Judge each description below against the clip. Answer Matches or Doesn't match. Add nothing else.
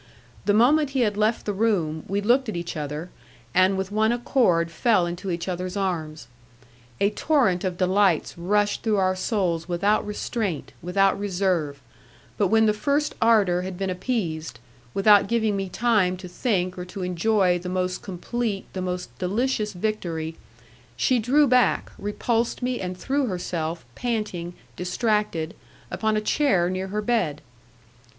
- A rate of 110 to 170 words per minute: Matches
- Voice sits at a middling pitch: Doesn't match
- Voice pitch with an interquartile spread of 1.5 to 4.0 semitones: Matches